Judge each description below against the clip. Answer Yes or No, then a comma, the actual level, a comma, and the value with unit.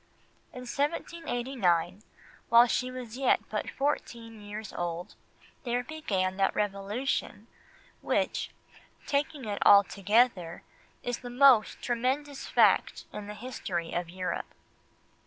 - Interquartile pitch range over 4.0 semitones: Yes, average, 4.6 semitones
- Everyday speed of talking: No, slow, 110 wpm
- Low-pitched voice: No, high, 230 Hz